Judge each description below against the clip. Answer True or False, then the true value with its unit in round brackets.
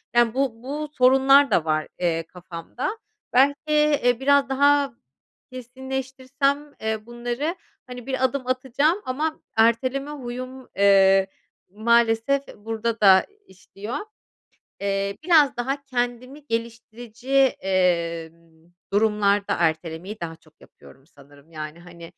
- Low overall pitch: False (240 Hz)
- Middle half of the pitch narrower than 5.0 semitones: False (5.5 semitones)